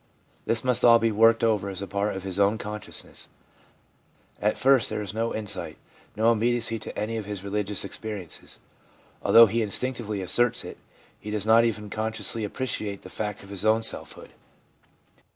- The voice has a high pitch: No, low, 110 Hz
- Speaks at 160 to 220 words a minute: Yes, average, 170 wpm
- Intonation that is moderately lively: No, narrow, 2.1 semitones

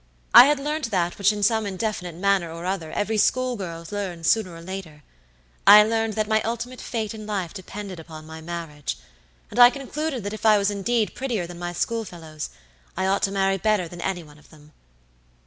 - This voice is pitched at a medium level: No, high, 195 Hz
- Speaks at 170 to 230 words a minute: Yes, average, 200 wpm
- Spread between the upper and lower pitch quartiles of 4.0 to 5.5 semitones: Yes, average, 4.3 semitones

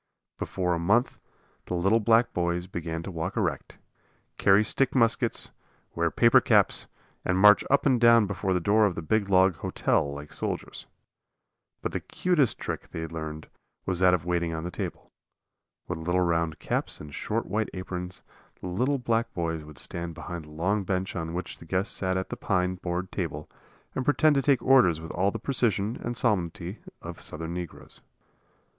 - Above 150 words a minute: Yes, average, 180 wpm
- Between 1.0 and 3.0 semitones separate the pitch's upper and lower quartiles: No, average, 4.4 semitones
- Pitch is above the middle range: No, very low, 90 Hz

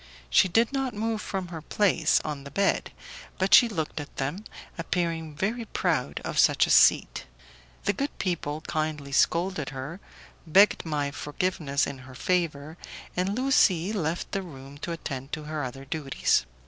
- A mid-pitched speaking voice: Yes, medium, 165 Hz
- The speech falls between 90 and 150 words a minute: No, average, 160 wpm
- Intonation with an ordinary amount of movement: Yes, average, 5.0 semitones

